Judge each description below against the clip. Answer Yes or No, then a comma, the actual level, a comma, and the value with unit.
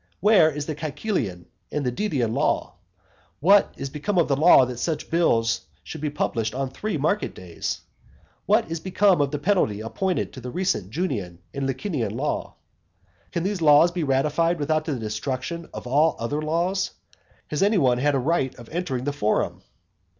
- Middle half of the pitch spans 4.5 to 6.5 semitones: Yes, average, 5.3 semitones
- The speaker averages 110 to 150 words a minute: No, average, 175 wpm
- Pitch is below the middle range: No, medium, 150 Hz